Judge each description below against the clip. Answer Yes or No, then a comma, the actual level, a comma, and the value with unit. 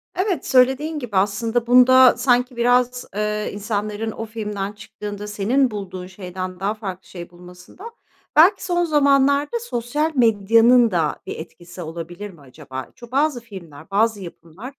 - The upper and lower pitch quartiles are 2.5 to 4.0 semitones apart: No, average, 5.0 semitones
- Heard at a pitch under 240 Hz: Yes, high, 220 Hz